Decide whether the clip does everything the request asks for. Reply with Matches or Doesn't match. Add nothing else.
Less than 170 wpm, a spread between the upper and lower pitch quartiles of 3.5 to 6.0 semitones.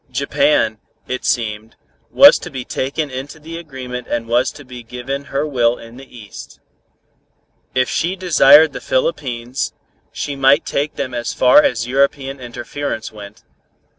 Doesn't match